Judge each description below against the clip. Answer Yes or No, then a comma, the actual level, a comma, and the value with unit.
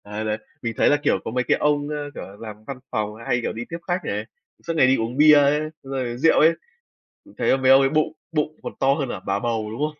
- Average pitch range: Yes, average, 4.9 semitones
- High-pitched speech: No, low, 135 Hz